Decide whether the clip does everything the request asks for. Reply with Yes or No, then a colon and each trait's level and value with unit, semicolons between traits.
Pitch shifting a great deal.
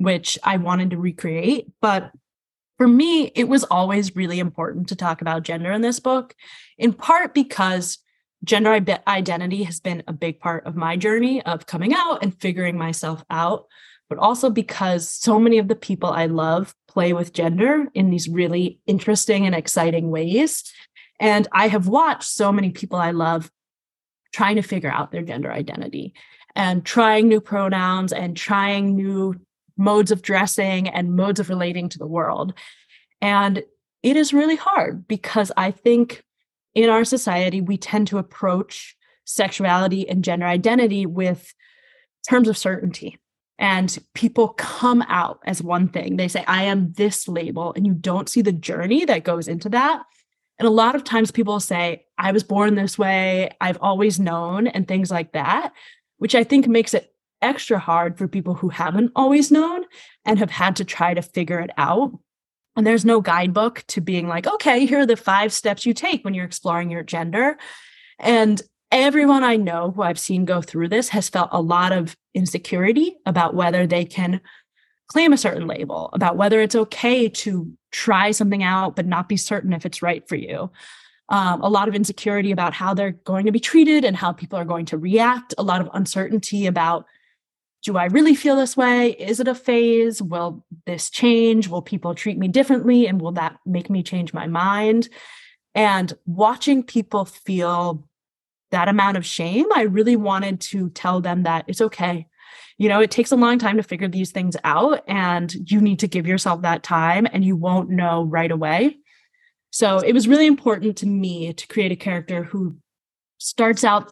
No: average, 4.3 semitones